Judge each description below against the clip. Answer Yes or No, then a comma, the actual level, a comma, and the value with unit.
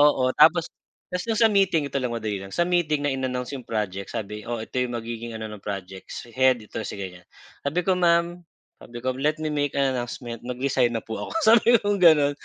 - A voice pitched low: Yes, low, 130 Hz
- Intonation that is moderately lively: No, wide, 5.8 semitones